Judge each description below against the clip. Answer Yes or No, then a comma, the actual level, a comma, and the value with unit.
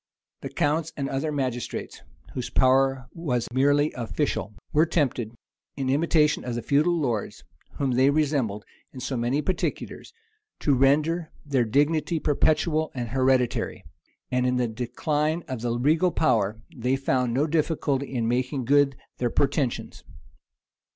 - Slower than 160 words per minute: Yes, average, 140 wpm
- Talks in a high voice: No, low, 135 Hz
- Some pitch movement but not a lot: Yes, average, 3.4 semitones